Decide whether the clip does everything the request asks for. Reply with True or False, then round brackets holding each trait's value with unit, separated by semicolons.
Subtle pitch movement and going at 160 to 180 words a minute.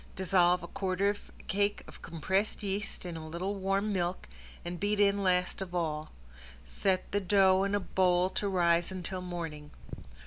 True (2.3 semitones; 175 wpm)